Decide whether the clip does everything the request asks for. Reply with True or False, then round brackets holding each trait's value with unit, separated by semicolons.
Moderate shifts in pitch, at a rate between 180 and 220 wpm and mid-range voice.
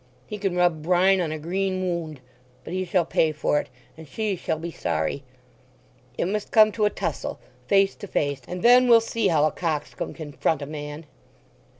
True (4.1 semitones; 195 wpm; 175 Hz)